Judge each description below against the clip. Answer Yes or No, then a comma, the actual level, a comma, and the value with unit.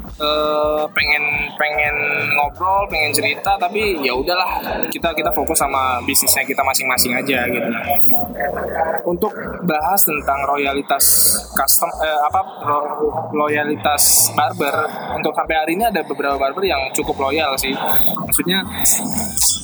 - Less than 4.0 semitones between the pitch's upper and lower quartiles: Yes, average, 2.8 semitones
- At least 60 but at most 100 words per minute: No, average, 120 wpm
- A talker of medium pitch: Yes, medium, 150 Hz